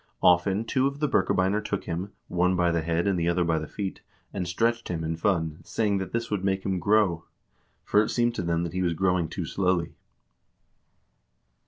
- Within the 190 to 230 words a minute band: Yes, fast, 205 wpm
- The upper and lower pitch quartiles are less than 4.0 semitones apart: Yes, average, 3.2 semitones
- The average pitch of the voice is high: No, very low, 90 Hz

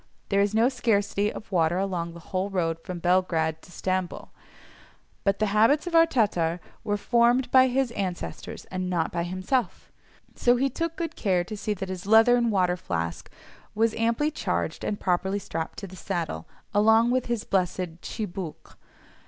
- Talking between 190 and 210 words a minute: No, average, 170 wpm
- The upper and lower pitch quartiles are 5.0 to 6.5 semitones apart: No, average, 4.6 semitones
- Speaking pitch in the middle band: No, high, 195 Hz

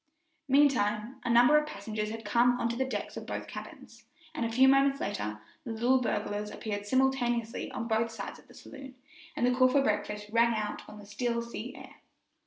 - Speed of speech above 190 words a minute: Yes, average, 200 wpm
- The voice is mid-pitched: No, high, 235 Hz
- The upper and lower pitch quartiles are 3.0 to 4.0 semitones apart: Yes, average, 3.5 semitones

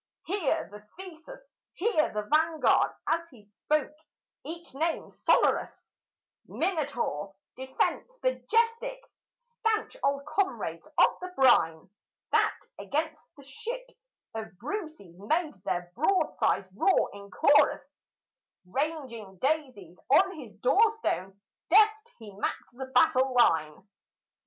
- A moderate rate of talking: No, slow, 110 wpm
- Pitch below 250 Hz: No, very high, 305 Hz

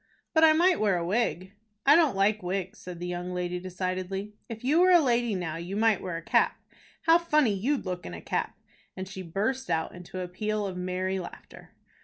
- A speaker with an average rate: No, fast, 215 wpm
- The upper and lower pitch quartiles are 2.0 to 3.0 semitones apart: No, average, 5.0 semitones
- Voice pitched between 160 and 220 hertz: Yes, high, 190 Hz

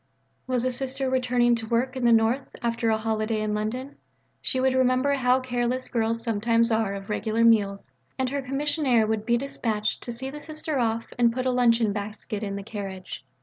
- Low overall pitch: No, high, 235 Hz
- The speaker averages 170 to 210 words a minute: Yes, average, 195 wpm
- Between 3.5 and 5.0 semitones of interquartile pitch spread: No, average, 2.8 semitones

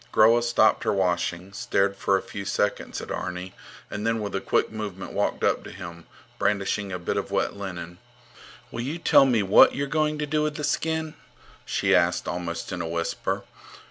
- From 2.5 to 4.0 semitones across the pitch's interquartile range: No, average, 4.8 semitones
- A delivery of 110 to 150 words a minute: No, average, 195 wpm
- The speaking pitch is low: Yes, low, 100 Hz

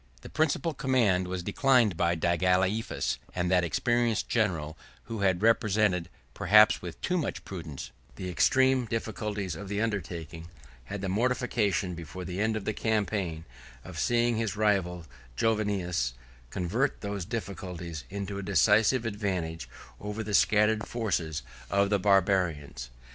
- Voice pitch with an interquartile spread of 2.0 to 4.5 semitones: Yes, average, 3.9 semitones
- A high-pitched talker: No, low, 100 Hz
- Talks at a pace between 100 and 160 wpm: Yes, average, 140 wpm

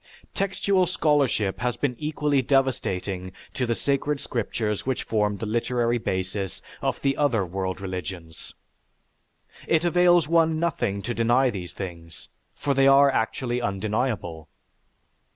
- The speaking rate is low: Yes, slow, 130 wpm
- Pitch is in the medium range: No, low, 120 Hz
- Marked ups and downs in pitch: Yes, wide, 6.4 semitones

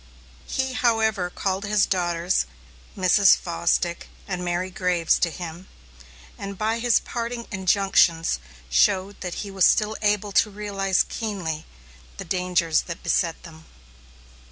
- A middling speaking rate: No, slow, 130 wpm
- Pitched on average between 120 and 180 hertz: No, high, 190 Hz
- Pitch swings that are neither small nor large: Yes, average, 3.2 semitones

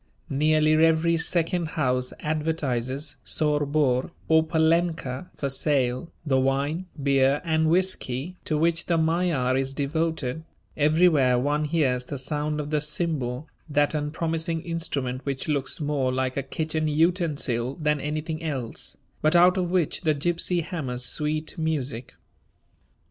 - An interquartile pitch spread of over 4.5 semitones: No, average, 3.2 semitones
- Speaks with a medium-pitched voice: Yes, medium, 150 Hz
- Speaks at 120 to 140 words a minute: Yes, slow, 135 wpm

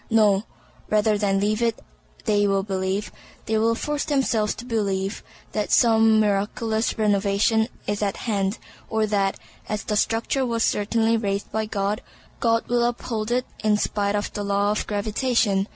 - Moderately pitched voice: No, high, 215 Hz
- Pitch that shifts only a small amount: Yes, narrow, 2.0 semitones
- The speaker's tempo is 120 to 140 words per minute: No, average, 160 wpm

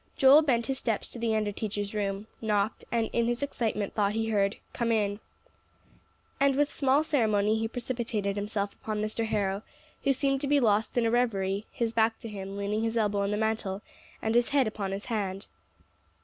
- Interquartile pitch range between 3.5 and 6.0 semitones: No, narrow, 2.6 semitones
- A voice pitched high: Yes, high, 220 Hz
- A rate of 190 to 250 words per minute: Yes, average, 195 wpm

